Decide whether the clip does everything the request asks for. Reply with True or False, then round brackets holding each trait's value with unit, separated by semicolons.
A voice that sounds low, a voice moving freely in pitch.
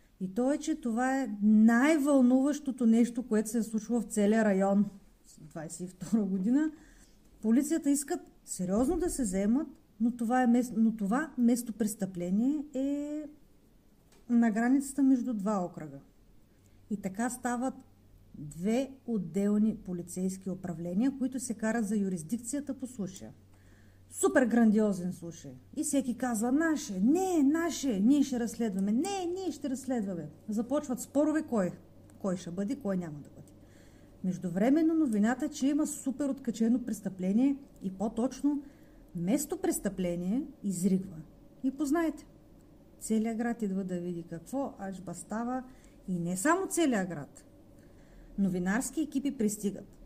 False (230 Hz; 5.9 semitones)